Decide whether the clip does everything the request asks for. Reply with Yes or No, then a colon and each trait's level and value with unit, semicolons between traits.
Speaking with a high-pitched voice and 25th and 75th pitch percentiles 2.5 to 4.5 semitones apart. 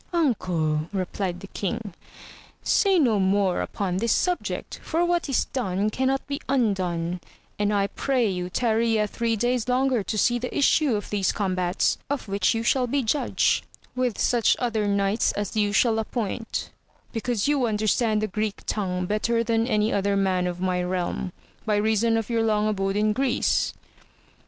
Yes: high, 215 Hz; average, 3.7 semitones